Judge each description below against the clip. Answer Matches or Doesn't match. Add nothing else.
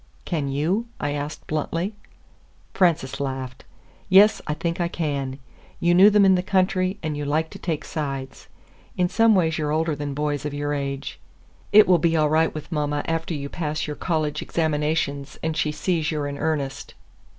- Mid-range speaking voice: Matches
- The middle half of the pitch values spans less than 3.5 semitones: Matches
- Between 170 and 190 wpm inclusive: Matches